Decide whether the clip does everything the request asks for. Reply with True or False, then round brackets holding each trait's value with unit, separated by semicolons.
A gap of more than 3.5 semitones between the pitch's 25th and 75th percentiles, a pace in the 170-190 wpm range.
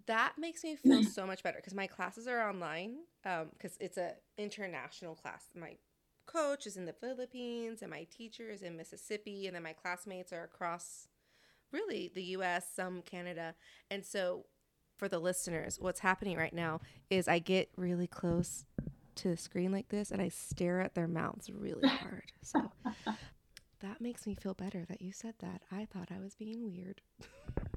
False (3.2 semitones; 180 wpm)